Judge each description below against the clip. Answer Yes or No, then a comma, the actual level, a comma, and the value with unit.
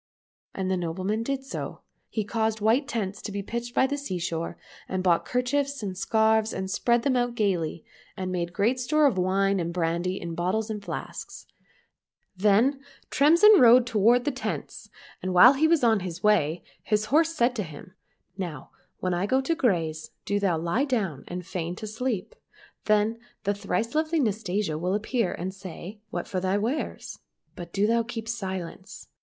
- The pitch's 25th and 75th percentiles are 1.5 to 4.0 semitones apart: No, average, 4.8 semitones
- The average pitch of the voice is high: Yes, high, 210 Hz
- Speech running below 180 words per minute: No, average, 185 wpm